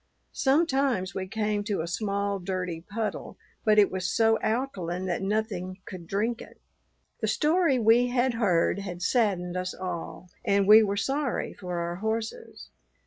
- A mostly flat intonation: No, average, 3.8 semitones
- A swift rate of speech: No, average, 155 wpm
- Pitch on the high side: Yes, high, 200 Hz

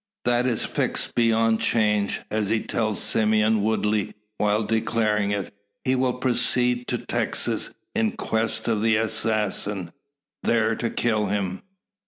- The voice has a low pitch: Yes, low, 110 Hz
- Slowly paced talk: Yes, slow, 130 wpm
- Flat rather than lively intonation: Yes, narrow, 1.7 semitones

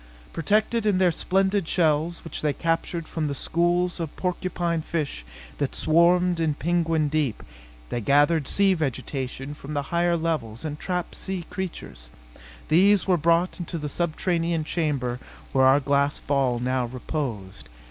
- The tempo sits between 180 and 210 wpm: No, average, 145 wpm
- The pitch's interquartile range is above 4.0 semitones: No, average, 3.7 semitones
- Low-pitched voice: No, medium, 160 Hz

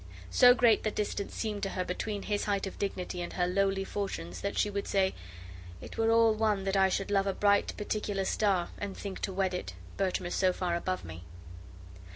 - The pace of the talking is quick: Yes, fast, 210 wpm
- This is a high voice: Yes, high, 195 Hz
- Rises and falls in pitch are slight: Yes, narrow, 1.9 semitones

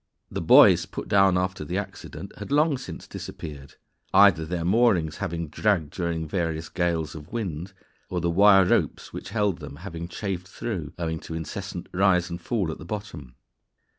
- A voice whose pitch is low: Yes, very low, 85 Hz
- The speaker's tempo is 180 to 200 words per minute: No, average, 170 wpm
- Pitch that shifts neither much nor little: Yes, average, 3.5 semitones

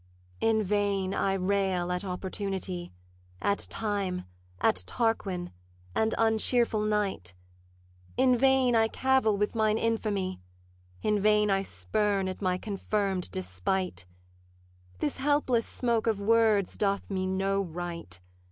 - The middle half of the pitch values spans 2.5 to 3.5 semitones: Yes, average, 3.0 semitones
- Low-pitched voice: No, high, 200 Hz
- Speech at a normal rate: No, slow, 120 wpm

